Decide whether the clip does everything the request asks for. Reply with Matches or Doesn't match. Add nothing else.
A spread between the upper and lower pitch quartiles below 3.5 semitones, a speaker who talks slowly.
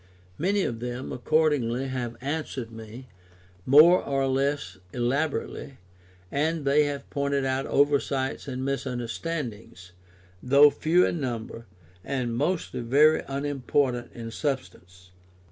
Matches